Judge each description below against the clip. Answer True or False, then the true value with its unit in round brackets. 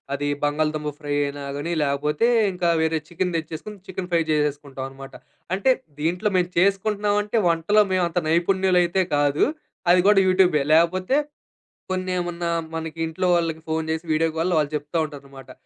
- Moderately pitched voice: True (165 Hz)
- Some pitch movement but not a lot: True (3.6 semitones)